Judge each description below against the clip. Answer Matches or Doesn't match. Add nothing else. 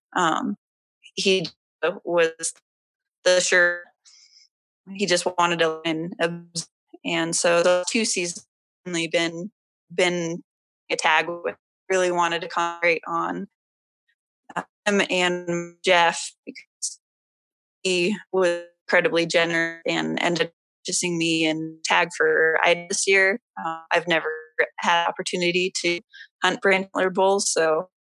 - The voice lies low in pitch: Doesn't match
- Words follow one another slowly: Matches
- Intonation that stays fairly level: Matches